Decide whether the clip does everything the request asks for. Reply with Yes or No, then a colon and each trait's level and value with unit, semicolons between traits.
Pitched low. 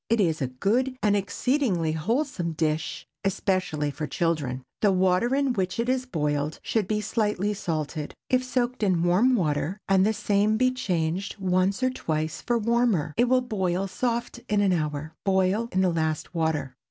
No: high, 190 Hz